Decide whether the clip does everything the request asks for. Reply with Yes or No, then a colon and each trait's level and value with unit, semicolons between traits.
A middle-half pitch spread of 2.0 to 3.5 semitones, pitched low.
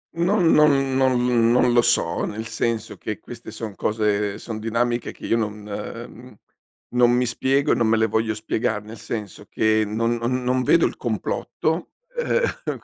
Yes: narrow, 2.6 semitones; low, 115 Hz